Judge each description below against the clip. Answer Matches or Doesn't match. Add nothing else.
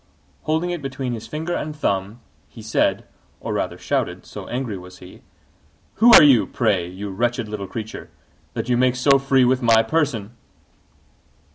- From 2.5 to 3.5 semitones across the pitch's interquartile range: Doesn't match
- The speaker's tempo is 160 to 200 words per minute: Matches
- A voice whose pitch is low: Matches